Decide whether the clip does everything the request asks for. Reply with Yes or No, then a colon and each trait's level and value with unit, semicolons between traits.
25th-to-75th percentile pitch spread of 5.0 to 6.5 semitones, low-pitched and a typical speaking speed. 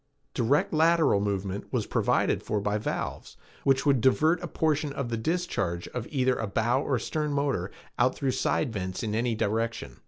Yes: average, 5.3 semitones; low, 125 Hz; average, 180 wpm